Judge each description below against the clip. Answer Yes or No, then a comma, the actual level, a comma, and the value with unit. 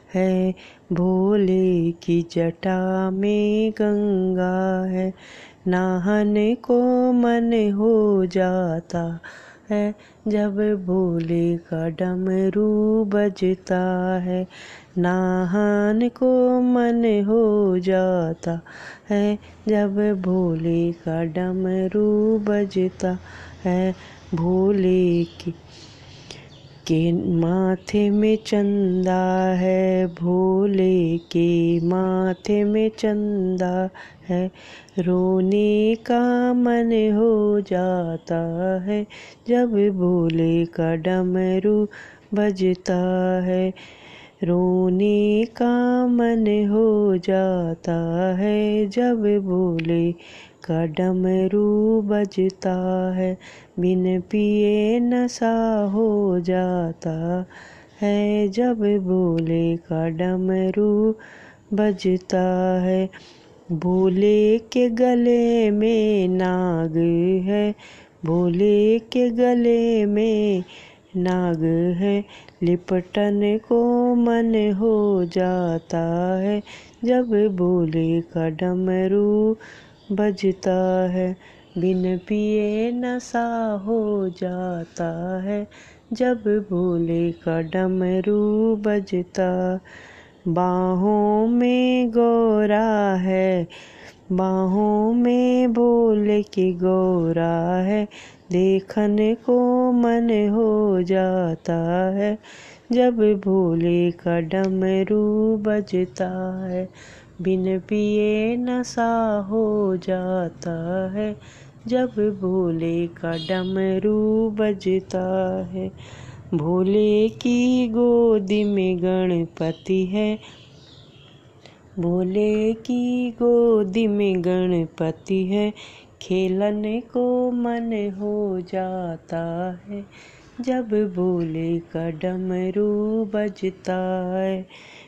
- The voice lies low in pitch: No, high, 190 Hz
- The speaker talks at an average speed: No, slow, 75 wpm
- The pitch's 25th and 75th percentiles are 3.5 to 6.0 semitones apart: No, narrow, 2.6 semitones